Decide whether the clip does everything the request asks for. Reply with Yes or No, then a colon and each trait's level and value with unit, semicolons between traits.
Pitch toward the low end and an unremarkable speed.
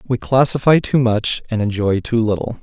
Yes: low, 115 Hz; average, 185 wpm